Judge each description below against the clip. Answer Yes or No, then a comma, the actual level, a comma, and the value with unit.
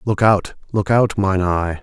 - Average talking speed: Yes, average, 195 wpm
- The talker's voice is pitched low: Yes, low, 100 Hz